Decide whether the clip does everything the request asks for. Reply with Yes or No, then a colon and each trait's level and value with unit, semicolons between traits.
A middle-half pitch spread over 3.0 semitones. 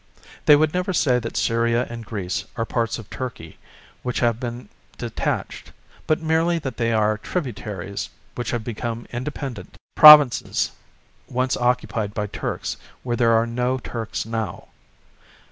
No: narrow, 2.4 semitones